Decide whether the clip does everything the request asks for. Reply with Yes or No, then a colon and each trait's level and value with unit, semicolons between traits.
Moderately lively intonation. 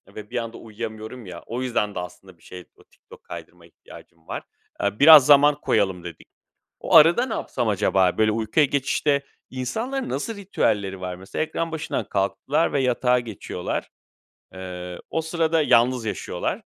No: wide, 7.3 semitones